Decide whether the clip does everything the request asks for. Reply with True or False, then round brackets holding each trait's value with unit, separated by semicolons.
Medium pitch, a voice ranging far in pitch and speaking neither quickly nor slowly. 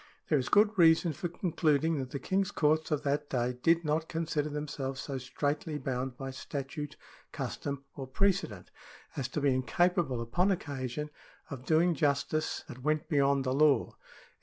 False (145 Hz; 3.3 semitones; 150 wpm)